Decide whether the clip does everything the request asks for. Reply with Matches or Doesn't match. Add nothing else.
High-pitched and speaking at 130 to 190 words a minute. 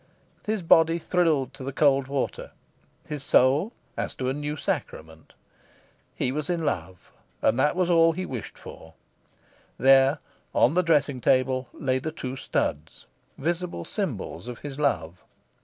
Doesn't match